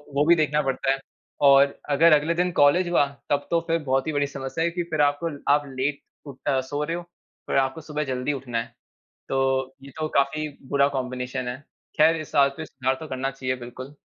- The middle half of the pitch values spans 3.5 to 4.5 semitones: No, narrow, 2.5 semitones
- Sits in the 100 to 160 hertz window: Yes, medium, 140 Hz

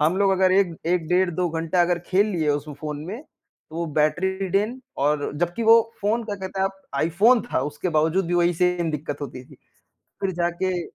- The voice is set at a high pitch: No, medium, 175 Hz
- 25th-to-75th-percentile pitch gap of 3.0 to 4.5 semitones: Yes, average, 3.5 semitones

